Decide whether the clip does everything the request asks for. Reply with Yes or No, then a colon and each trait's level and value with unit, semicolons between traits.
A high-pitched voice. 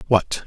No: low, 105 Hz